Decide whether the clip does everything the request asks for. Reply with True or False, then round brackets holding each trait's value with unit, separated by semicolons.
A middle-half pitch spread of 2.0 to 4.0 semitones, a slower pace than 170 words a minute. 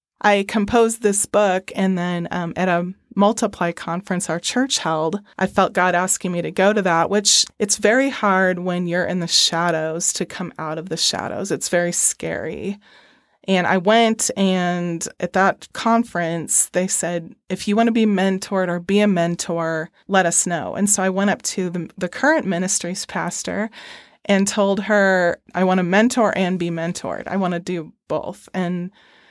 False (2.9 semitones; 185 wpm)